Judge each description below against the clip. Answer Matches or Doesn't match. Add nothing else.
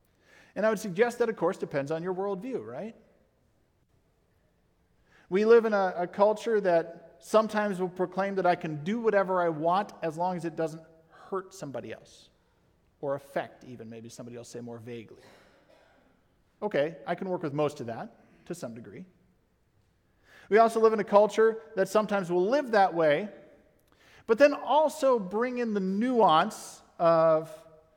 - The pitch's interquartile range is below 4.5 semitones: Doesn't match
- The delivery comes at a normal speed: Matches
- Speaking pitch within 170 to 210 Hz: Matches